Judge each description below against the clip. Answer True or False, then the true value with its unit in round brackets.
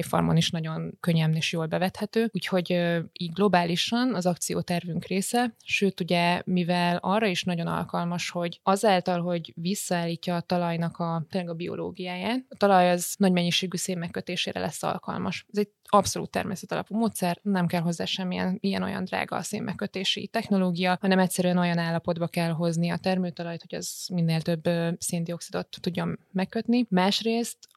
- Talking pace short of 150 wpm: False (155 wpm)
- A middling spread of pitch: False (2.1 semitones)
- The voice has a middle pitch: True (180 Hz)